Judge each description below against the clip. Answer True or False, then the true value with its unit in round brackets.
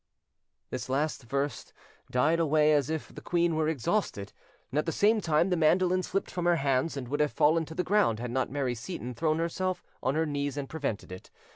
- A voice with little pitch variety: False (3.8 semitones)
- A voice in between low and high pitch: True (155 Hz)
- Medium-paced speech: False (215 wpm)